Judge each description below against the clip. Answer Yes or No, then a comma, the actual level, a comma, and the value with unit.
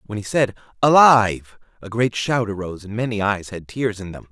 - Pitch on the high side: No, low, 110 Hz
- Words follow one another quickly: Yes, fast, 210 wpm